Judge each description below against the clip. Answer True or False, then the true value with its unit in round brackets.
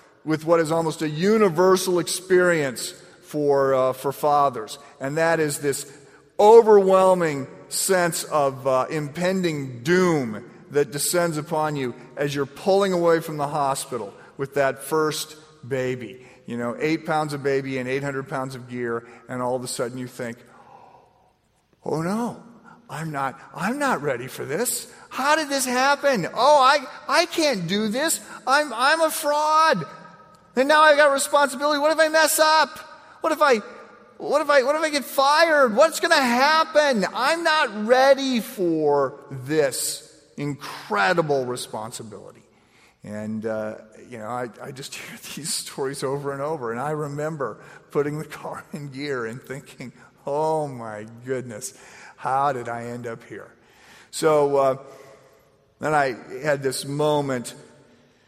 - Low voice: False (155 Hz)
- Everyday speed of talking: True (150 wpm)